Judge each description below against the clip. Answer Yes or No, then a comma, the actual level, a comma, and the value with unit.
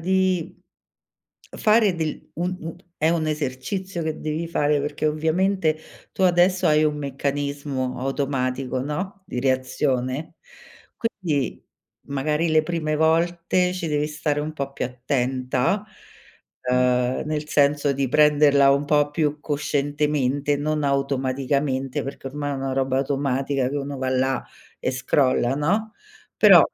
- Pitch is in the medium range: Yes, medium, 145 Hz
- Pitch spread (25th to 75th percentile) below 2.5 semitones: No, average, 2.8 semitones